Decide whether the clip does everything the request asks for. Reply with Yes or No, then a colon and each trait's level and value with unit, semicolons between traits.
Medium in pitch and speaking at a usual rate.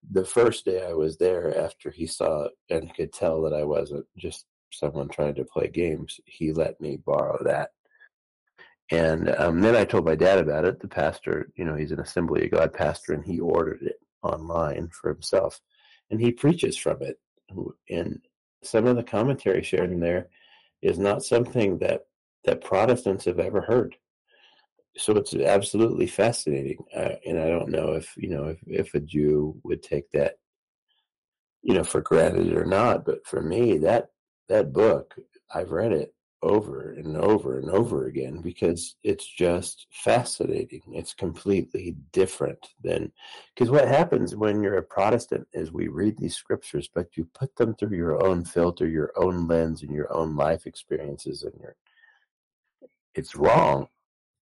No: low, 120 Hz; average, 170 wpm